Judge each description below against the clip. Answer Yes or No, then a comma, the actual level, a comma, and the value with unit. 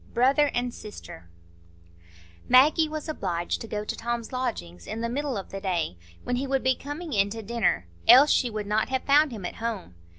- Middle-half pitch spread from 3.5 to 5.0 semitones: Yes, average, 4.6 semitones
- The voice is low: No, high, 235 Hz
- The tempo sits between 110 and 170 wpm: No, average, 200 wpm